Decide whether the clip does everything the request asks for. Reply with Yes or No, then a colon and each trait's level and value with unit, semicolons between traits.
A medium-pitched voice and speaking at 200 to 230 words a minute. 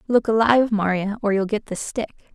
No: high, 215 Hz; fast, 205 wpm